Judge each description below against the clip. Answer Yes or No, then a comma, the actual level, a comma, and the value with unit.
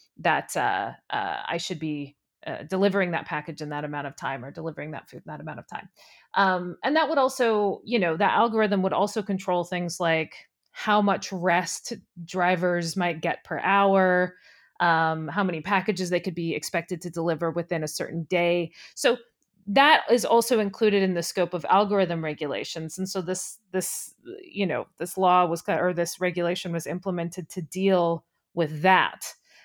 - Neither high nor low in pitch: Yes, medium, 180 Hz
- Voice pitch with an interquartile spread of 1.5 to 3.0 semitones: Yes, average, 2.7 semitones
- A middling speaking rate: Yes, average, 180 wpm